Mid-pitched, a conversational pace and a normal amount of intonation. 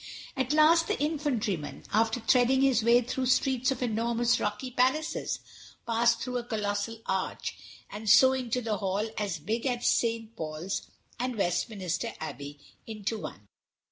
No: high, 230 Hz; average, 145 wpm; average, 3.7 semitones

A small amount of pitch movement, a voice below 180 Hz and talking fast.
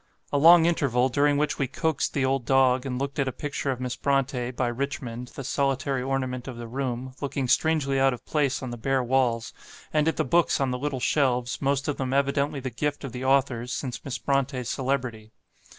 Yes: narrow, 1.8 semitones; low, 135 Hz; fast, 215 wpm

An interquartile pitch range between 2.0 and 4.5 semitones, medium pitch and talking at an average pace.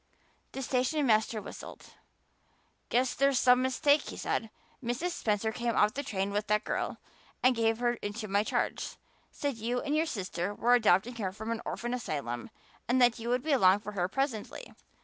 No: average, 3.5 semitones; high, 235 Hz; average, 180 wpm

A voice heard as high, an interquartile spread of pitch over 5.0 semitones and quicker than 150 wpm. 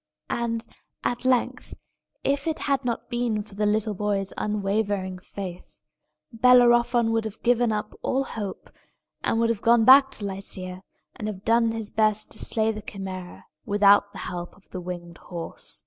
No: high, 215 Hz; average, 3.2 semitones; average, 165 wpm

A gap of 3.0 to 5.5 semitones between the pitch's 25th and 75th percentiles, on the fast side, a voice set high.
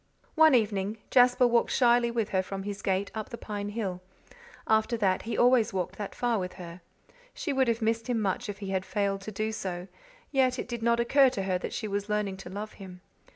Yes: average, 3.5 semitones; fast, 225 wpm; high, 215 Hz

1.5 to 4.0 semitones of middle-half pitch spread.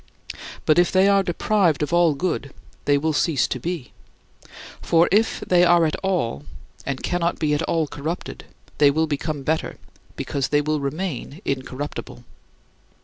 Yes: average, 3.4 semitones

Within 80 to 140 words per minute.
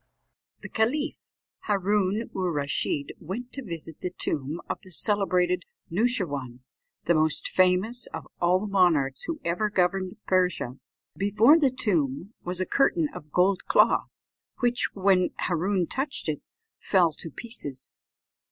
Yes: slow, 135 wpm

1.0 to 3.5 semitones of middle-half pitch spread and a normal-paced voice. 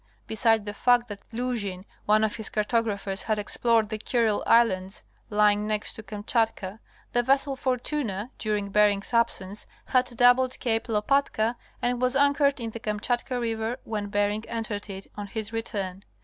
Yes: average, 2.7 semitones; average, 155 wpm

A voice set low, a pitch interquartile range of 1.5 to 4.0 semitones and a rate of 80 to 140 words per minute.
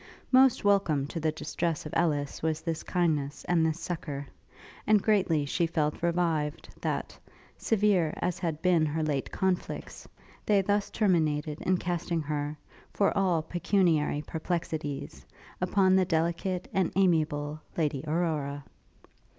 No: medium, 165 Hz; average, 3.2 semitones; slow, 135 wpm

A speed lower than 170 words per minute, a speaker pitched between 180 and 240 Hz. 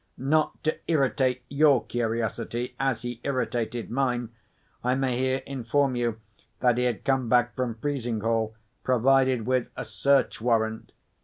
No: average, 140 wpm; low, 125 Hz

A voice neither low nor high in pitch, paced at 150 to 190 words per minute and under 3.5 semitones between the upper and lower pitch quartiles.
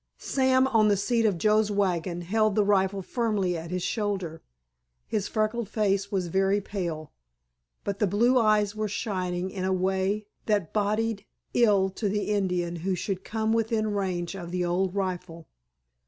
No: high, 200 Hz; average, 165 wpm; average, 2.7 semitones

